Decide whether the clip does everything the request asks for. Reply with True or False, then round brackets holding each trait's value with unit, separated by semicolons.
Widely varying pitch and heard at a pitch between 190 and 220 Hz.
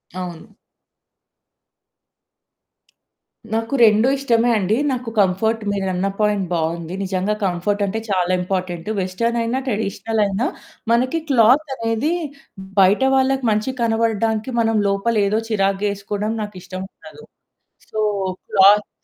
False (3.1 semitones; 210 Hz)